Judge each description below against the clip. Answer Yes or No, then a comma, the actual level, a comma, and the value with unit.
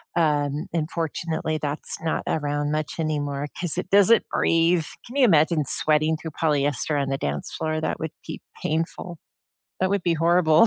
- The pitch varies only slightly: Yes, narrow, 2.3 semitones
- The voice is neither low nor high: Yes, medium, 160 Hz